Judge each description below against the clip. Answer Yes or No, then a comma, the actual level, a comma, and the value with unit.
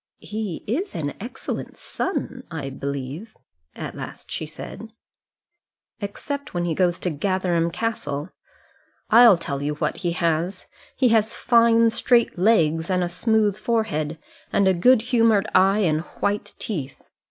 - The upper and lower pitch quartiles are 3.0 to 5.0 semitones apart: No, wide, 5.6 semitones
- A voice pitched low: No, high, 190 Hz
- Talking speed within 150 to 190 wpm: No, average, 140 wpm